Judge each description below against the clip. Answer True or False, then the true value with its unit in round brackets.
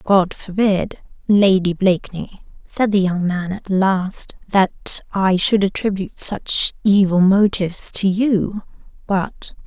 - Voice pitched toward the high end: True (195 Hz)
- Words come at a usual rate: False (125 wpm)